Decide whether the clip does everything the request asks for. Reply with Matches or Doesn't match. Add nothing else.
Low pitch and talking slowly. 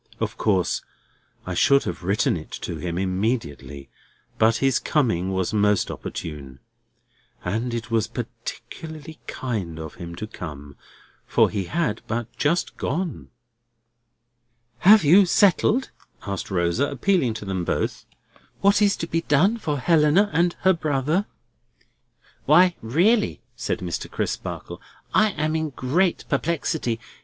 Matches